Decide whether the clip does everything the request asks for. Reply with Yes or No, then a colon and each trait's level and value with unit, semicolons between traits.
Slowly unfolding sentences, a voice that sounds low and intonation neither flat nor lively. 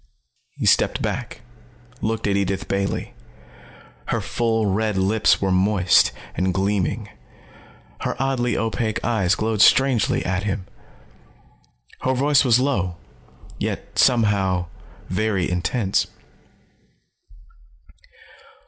Yes: slow, 100 wpm; low, 105 Hz; average, 3.4 semitones